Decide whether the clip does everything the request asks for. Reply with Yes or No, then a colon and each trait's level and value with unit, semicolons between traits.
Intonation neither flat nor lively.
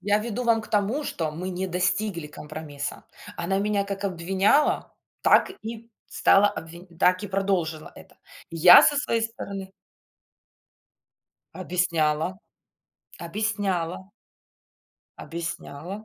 Yes: average, 3.6 semitones